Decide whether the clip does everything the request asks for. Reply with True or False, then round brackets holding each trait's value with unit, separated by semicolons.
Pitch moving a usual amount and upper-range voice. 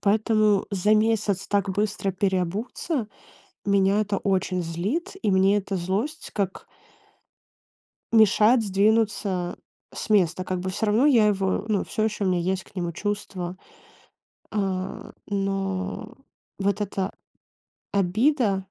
False (2.2 semitones; 200 Hz)